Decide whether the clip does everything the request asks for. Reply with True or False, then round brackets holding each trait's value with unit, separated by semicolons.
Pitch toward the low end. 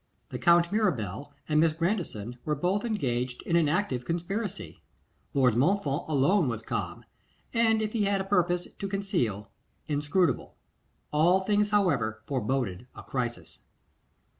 False (165 Hz)